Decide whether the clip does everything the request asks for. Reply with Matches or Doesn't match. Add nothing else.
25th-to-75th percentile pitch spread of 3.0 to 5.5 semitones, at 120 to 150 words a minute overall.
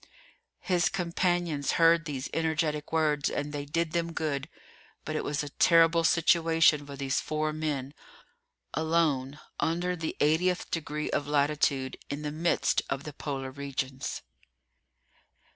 Doesn't match